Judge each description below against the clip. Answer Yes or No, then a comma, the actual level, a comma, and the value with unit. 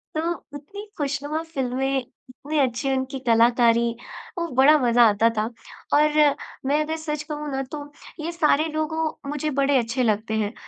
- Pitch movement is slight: No, average, 3.6 semitones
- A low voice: No, very high, 280 Hz